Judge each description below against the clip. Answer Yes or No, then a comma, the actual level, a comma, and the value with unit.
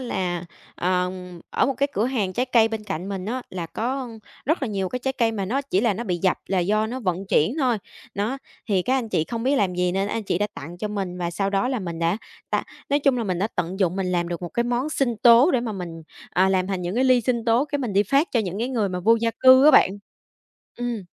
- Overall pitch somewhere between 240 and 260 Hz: No, high, 210 Hz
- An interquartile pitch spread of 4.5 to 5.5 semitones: Yes, average, 5.1 semitones